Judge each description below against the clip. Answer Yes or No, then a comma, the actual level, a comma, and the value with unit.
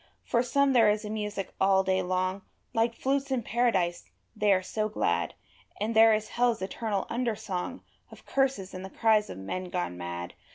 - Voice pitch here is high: Yes, high, 210 Hz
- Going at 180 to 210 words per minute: Yes, average, 190 wpm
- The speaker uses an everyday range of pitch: Yes, average, 3.9 semitones